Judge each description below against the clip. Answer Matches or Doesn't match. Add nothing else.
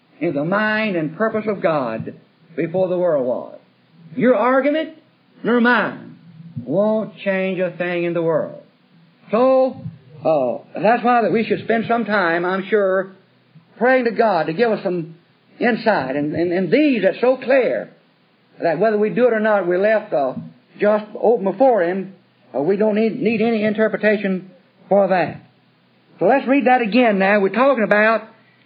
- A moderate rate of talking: Matches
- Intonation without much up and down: Doesn't match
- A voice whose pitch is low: Doesn't match